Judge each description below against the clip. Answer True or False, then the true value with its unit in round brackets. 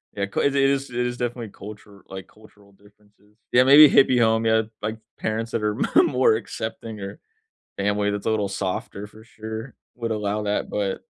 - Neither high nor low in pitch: False (110 Hz)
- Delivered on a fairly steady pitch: True (2.1 semitones)